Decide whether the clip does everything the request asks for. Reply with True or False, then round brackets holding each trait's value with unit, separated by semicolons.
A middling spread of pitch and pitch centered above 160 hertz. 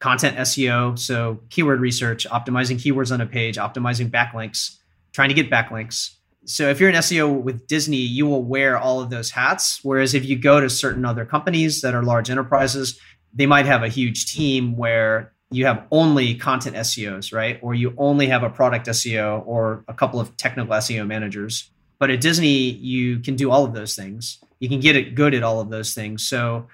False (3.0 semitones; 125 Hz)